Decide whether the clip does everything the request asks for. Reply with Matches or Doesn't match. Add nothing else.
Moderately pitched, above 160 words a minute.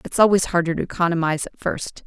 Matches